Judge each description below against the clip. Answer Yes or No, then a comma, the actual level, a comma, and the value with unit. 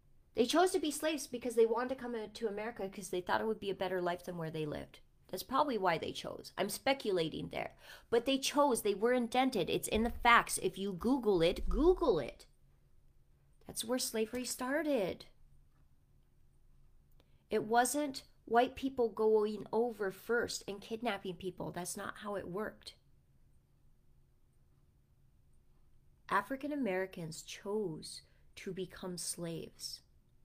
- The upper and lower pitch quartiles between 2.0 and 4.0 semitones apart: No, average, 4.7 semitones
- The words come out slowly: No, average, 145 wpm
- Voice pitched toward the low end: No, high, 220 Hz